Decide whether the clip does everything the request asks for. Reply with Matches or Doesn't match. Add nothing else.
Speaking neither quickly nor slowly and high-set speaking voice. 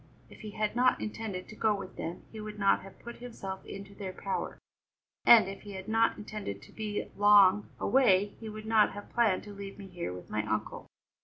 Doesn't match